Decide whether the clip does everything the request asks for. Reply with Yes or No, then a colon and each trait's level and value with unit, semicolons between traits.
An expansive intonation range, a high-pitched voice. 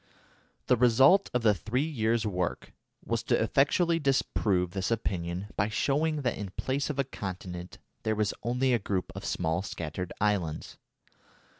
No: wide, 6.1 semitones; low, 110 Hz